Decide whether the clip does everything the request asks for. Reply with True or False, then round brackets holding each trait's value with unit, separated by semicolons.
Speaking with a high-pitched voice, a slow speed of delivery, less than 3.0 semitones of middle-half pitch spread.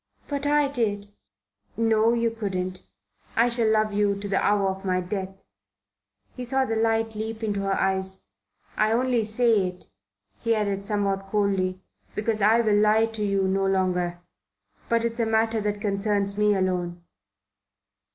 False (210 Hz; 160 wpm; 2.5 semitones)